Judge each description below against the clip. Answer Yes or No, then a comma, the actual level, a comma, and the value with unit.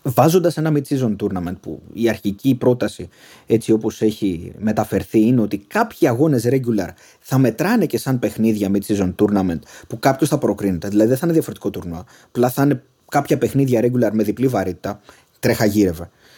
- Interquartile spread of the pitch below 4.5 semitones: No, average, 4.8 semitones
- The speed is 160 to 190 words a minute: Yes, average, 165 wpm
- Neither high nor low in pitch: No, low, 115 Hz